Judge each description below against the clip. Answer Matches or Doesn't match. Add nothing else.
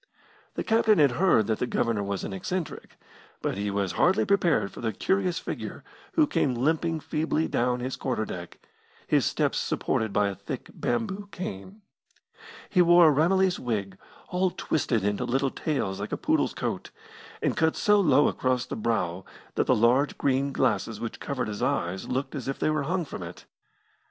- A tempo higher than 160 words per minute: Matches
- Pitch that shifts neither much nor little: Doesn't match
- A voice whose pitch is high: Doesn't match